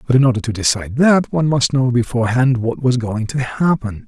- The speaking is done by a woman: No, male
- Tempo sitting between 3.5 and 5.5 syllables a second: No, 5.9 syllables/s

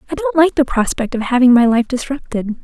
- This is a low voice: No, very high, 265 Hz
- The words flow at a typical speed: No, fast, 230 wpm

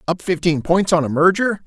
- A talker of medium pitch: Yes, medium, 175 Hz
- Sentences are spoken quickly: Yes, fast, 215 wpm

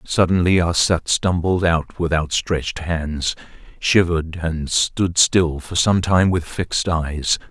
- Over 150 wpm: No, slow, 135 wpm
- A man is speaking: Yes, male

